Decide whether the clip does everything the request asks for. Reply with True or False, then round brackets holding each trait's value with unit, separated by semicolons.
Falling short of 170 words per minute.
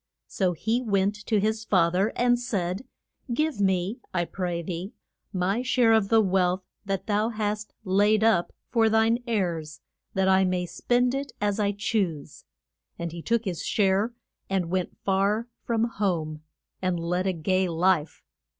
True (160 wpm)